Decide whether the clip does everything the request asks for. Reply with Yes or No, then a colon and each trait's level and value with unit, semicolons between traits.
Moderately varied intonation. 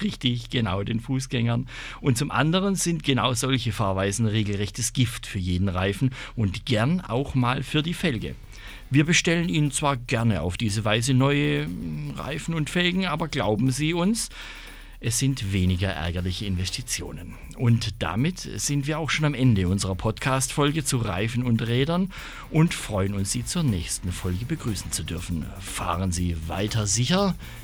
No: wide, 6.4 semitones